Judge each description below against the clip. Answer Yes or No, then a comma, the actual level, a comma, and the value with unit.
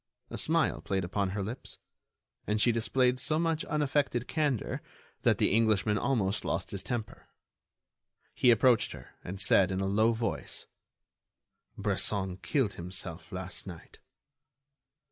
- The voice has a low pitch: Yes, low, 105 Hz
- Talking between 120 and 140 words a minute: Yes, slow, 135 wpm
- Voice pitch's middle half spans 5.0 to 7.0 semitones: No, average, 4.5 semitones